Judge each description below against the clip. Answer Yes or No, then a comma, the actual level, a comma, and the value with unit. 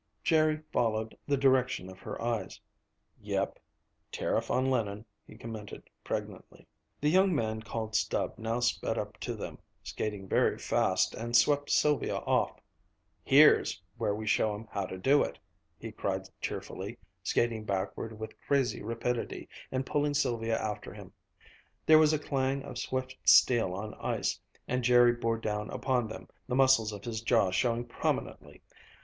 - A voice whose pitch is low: Yes, low, 115 Hz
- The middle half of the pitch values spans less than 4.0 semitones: Yes, average, 3.4 semitones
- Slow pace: No, average, 155 wpm